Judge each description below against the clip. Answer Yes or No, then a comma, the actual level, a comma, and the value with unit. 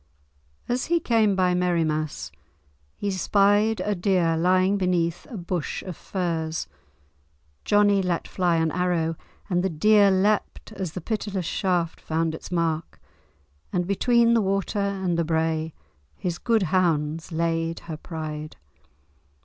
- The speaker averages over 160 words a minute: No, slow, 135 wpm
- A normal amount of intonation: Yes, average, 3.3 semitones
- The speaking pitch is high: No, medium, 180 Hz